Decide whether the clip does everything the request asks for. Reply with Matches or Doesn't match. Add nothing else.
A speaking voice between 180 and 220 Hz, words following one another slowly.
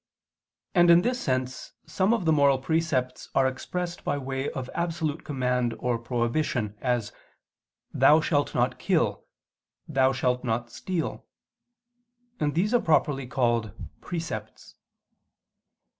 Doesn't match